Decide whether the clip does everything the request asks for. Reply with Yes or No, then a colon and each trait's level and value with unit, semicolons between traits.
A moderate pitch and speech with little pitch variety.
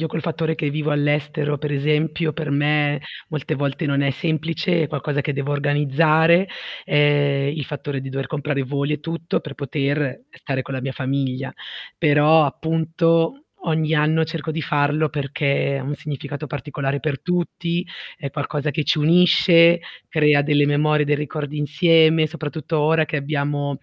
Yes: medium, 150 Hz; narrow, 2.0 semitones